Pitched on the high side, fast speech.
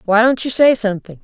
Yes: high, 225 Hz; fast, 245 wpm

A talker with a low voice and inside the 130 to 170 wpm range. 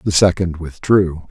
Yes: very low, 90 Hz; average, 140 wpm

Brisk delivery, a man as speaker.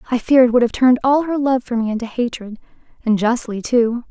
No: fast, 235 wpm; female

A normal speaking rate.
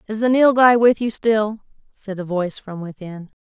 Yes: average, 195 wpm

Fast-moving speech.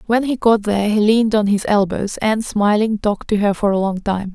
Yes: fast, 250 wpm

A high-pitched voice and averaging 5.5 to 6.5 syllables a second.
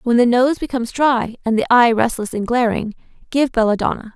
Yes: high, 240 Hz; 5.7 syllables/s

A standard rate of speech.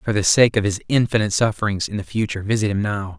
No: fast, 245 wpm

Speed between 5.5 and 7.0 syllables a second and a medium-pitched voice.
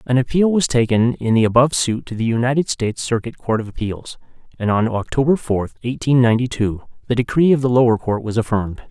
No: 6.1 syllables/s; low, 120 Hz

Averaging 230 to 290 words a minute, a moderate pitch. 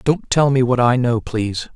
No: fast, 240 wpm; low, 125 Hz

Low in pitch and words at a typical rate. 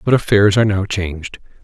Yes: low, 100 Hz; average, 185 wpm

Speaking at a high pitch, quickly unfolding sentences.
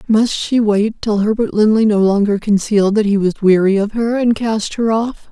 Yes: high, 215 Hz; fast, 215 wpm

